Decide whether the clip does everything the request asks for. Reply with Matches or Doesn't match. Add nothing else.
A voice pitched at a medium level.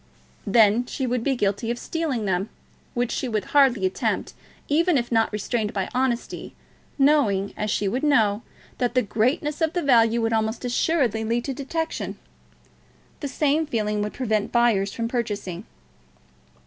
Doesn't match